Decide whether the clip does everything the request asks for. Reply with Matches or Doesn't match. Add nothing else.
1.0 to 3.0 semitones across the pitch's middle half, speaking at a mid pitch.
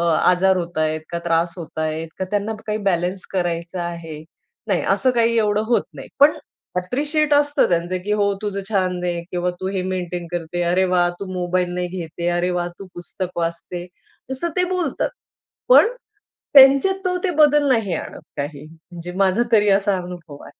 Doesn't match